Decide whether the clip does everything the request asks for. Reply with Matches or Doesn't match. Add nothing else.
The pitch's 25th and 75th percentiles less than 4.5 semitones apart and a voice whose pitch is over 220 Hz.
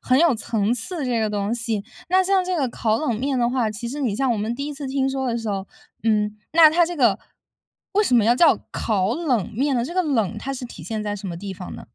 Doesn't match